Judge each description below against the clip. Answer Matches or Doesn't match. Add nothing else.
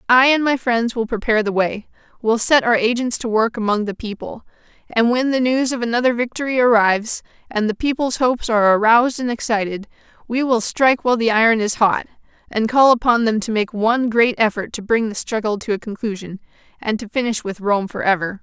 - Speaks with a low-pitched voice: Doesn't match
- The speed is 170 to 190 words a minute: Doesn't match